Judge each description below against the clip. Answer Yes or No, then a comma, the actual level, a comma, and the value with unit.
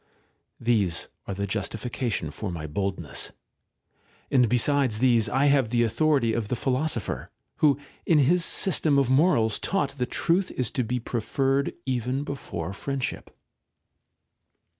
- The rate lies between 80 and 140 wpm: Yes, slow, 135 wpm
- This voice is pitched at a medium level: No, low, 125 Hz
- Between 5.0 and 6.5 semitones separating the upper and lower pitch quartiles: No, average, 4.3 semitones